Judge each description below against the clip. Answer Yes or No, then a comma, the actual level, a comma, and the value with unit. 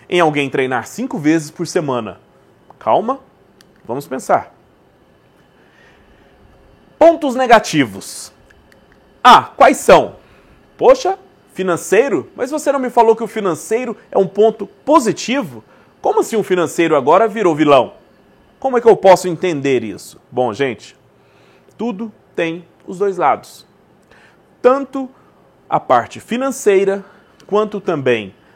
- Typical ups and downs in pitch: No, wide, 7.0 semitones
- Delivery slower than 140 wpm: Yes, slow, 120 wpm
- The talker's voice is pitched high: Yes, high, 200 Hz